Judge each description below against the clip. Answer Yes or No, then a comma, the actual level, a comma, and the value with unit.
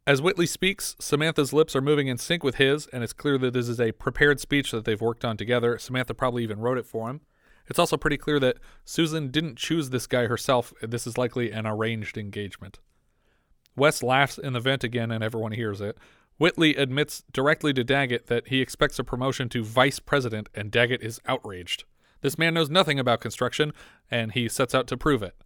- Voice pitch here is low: Yes, low, 130 Hz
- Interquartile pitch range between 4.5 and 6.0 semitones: No, average, 3.8 semitones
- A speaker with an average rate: No, fast, 210 wpm